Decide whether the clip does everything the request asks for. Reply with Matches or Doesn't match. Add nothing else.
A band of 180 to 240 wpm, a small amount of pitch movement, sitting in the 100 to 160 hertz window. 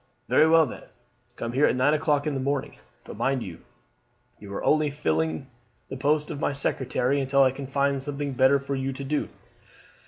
Matches